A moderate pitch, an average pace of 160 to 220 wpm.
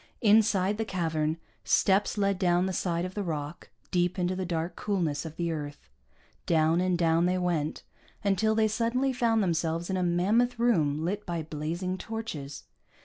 Yes: medium, 180 Hz; average, 170 wpm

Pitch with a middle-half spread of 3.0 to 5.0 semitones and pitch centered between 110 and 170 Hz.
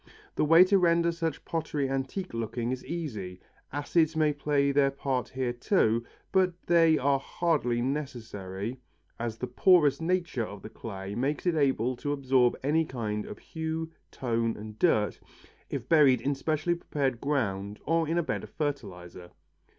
No: wide, 5.6 semitones; medium, 140 Hz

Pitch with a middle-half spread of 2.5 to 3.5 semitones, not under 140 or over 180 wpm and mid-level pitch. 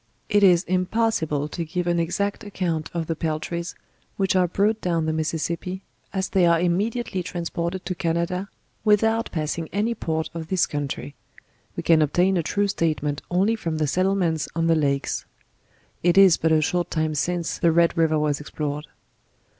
Yes: average, 3.1 semitones; average, 175 wpm; medium, 170 Hz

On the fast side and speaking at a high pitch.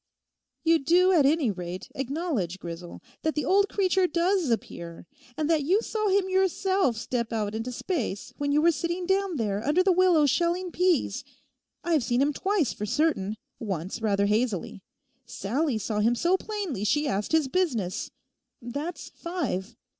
No: average, 160 wpm; very high, 295 Hz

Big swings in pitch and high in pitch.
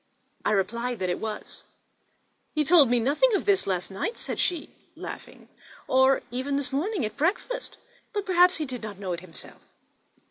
Yes: wide, 8.7 semitones; very high, 265 Hz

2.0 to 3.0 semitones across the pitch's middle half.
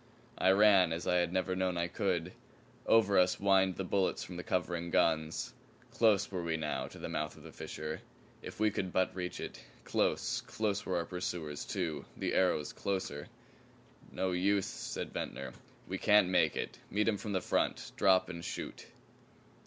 Yes: narrow, 2.4 semitones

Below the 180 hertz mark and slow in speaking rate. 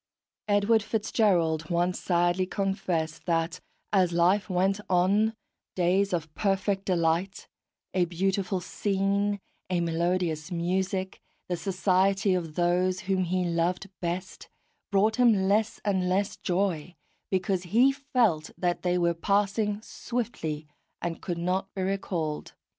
No: medium, 185 Hz; slow, 125 wpm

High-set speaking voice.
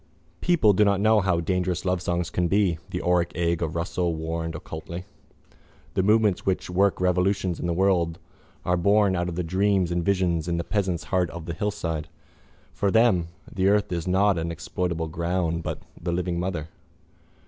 No: very low, 90 Hz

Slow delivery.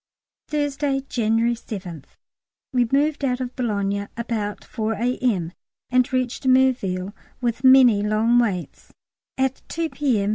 Yes: slow, 120 wpm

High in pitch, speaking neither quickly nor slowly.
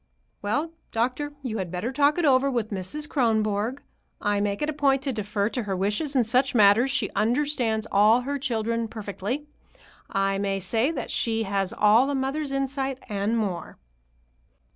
Yes: high, 230 Hz; average, 170 wpm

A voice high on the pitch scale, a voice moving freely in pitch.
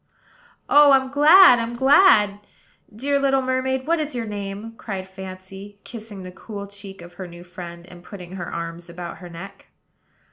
Yes: high, 200 Hz; wide, 6.2 semitones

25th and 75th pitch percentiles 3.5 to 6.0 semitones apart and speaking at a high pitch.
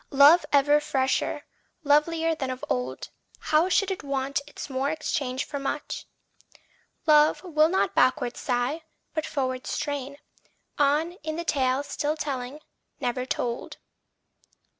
No: average, 2.9 semitones; very high, 285 Hz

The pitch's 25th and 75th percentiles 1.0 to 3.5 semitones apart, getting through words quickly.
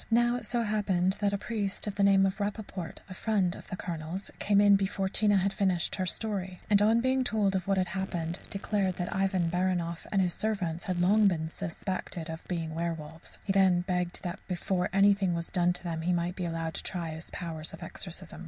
Yes: narrow, 2.6 semitones; fast, 215 wpm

